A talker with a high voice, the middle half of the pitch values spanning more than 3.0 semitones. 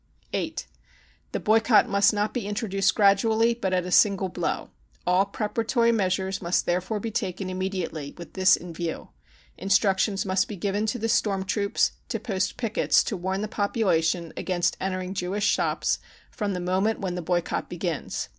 No: high, 195 Hz; narrow, 2.5 semitones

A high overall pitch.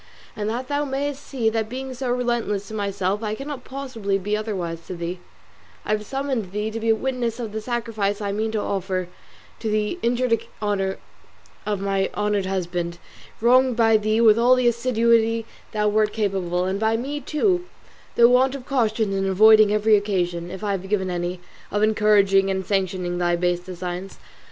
Yes: high, 215 Hz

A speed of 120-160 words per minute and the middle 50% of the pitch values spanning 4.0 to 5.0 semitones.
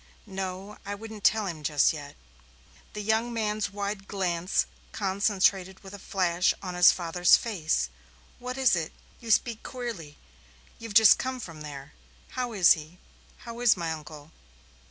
Yes: average, 155 wpm; average, 4.6 semitones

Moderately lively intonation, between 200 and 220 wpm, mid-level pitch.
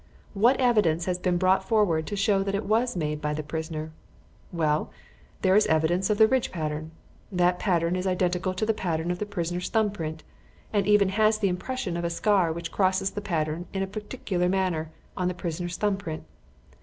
Yes: average, 3.6 semitones; fast, 205 wpm; medium, 180 Hz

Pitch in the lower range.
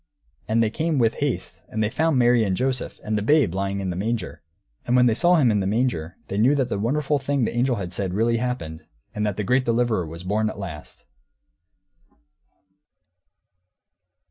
Yes: low, 115 Hz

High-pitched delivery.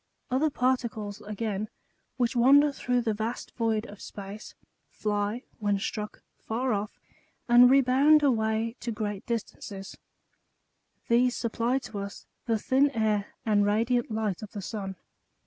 Yes: high, 225 Hz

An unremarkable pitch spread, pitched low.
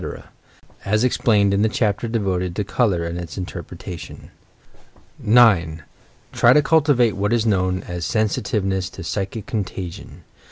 Yes: average, 3.6 semitones; low, 100 Hz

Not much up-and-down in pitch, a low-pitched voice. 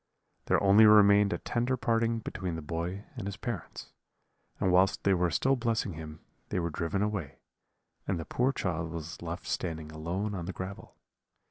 No: average, 4.2 semitones; very low, 95 Hz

